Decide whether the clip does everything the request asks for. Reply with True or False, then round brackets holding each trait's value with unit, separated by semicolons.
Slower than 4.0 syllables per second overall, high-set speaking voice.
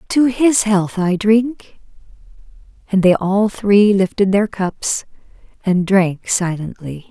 True (3.5 syllables/s; 200 Hz)